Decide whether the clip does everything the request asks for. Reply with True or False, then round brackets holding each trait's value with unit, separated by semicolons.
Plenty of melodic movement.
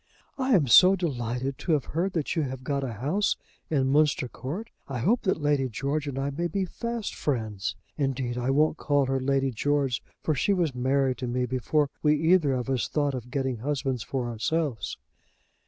False (3.4 semitones)